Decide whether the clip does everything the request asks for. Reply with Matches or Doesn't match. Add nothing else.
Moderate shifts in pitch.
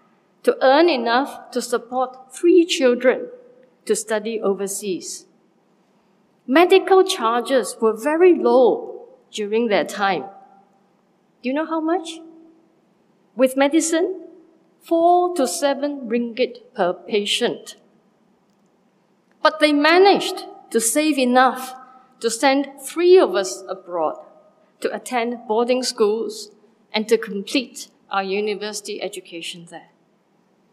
Doesn't match